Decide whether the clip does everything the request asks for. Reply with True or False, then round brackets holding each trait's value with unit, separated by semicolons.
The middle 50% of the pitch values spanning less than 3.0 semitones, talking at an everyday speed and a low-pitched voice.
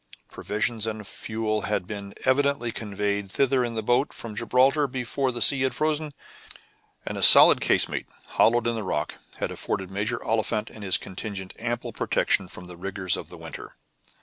False (3.7 semitones; 175 wpm; 115 Hz)